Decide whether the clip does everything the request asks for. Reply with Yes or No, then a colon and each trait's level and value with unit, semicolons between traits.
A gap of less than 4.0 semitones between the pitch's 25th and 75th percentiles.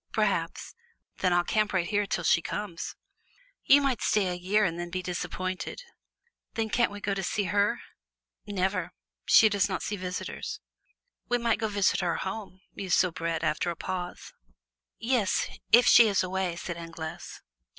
Yes: average, 2.9 semitones